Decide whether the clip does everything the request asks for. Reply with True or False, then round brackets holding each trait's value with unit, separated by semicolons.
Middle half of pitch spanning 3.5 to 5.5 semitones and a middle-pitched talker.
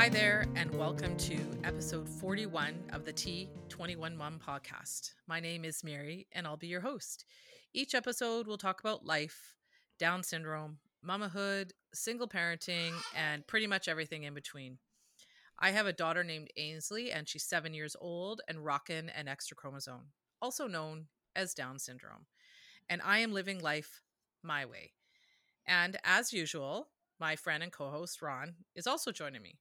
True (4.4 semitones; 165 Hz)